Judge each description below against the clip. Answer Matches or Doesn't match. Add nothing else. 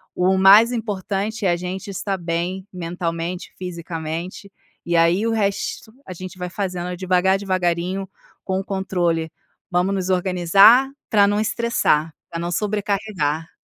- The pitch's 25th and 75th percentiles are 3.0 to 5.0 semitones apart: Doesn't match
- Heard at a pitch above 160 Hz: Matches